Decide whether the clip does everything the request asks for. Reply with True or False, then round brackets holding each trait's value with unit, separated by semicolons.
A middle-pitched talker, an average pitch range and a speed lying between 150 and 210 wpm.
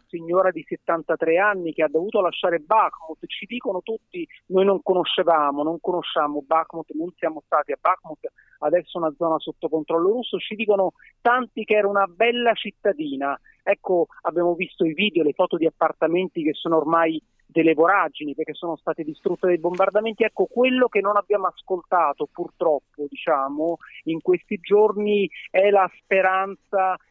True (175 Hz; 4.1 semitones; 155 wpm)